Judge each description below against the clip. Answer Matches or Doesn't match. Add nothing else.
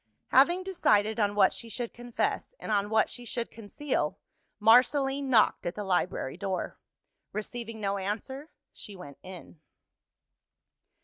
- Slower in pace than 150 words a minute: Matches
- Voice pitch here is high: Matches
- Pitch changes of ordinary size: Matches